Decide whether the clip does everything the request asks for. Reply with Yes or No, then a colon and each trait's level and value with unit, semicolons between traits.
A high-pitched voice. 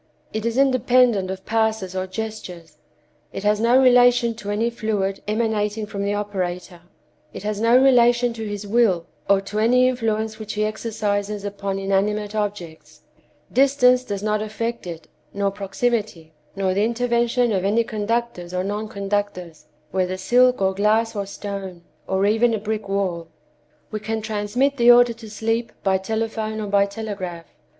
Yes: high, 210 Hz